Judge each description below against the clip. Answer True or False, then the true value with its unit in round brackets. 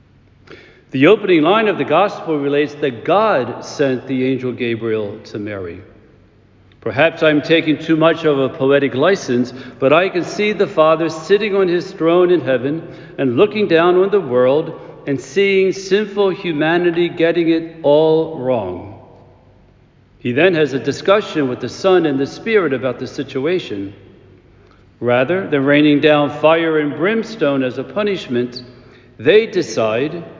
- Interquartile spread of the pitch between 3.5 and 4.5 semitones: False (5.6 semitones)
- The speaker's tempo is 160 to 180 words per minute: False (150 wpm)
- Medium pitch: True (150 Hz)